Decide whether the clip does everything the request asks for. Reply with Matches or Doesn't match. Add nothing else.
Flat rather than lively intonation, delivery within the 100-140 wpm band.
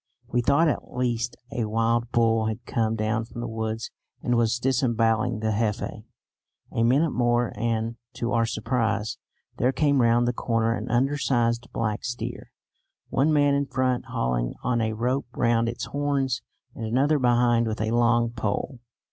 Doesn't match